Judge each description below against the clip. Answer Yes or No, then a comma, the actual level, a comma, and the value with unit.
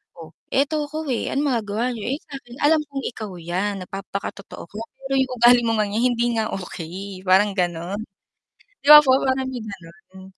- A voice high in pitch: Yes, high, 215 Hz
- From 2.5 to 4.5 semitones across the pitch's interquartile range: No, wide, 5.6 semitones